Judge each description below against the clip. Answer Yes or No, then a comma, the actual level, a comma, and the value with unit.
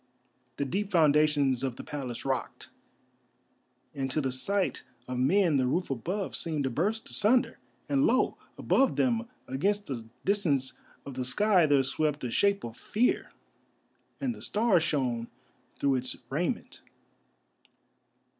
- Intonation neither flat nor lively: No, wide, 7.3 semitones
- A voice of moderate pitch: Yes, medium, 150 Hz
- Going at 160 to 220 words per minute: No, average, 140 wpm